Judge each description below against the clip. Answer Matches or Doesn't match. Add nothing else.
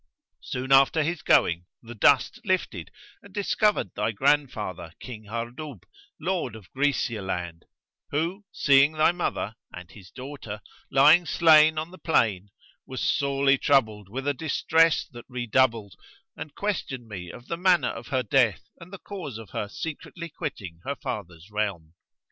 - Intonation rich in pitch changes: Matches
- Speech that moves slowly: Doesn't match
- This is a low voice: Matches